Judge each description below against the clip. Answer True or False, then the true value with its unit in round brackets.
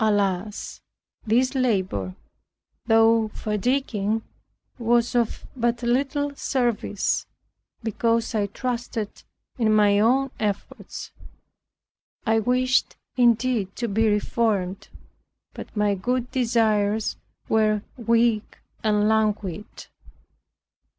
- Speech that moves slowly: True (90 wpm)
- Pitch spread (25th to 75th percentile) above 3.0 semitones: False (2.6 semitones)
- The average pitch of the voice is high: True (225 Hz)